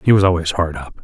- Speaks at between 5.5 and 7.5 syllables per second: Yes, 6.5 syllables/s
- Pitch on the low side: Yes, very low, 85 Hz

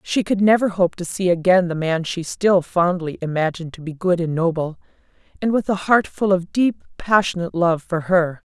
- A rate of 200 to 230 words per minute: Yes, fast, 205 wpm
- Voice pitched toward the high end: No, medium, 180 Hz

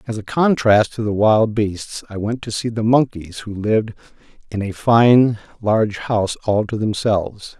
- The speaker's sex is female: No, male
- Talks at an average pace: Yes, average, 180 wpm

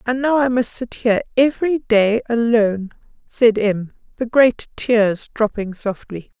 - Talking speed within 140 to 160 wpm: Yes, average, 150 wpm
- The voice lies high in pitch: Yes, high, 230 Hz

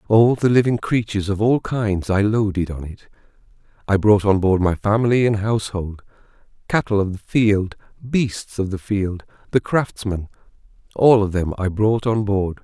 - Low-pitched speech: Yes, low, 105 Hz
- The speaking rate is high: No, average, 170 wpm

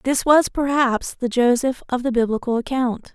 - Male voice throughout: No, female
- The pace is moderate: Yes, average, 170 wpm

